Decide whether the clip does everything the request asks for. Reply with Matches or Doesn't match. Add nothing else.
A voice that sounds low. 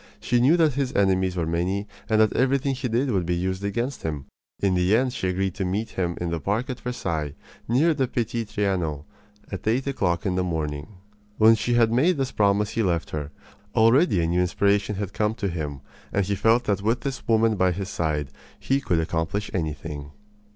Matches